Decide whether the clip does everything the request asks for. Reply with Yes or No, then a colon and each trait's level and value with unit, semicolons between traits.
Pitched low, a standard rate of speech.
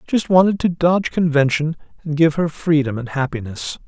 No: medium, 155 Hz; average, 170 wpm